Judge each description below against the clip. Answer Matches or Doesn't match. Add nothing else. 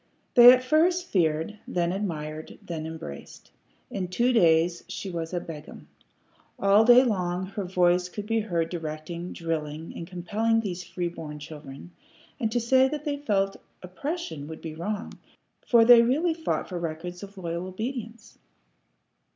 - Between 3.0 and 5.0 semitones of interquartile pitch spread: Doesn't match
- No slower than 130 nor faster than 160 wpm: Matches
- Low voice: Doesn't match